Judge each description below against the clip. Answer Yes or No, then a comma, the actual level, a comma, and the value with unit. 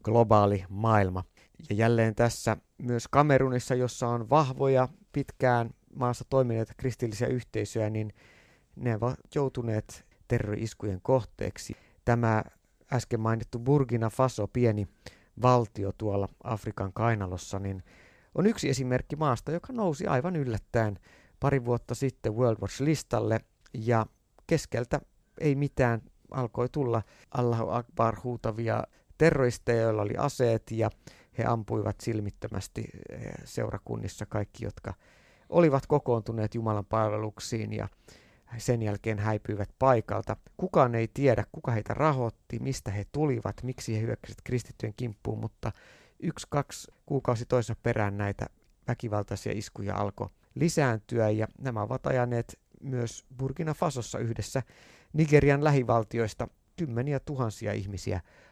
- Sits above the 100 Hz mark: Yes, low, 115 Hz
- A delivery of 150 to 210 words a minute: No, average, 115 wpm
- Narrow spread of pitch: No, average, 3.4 semitones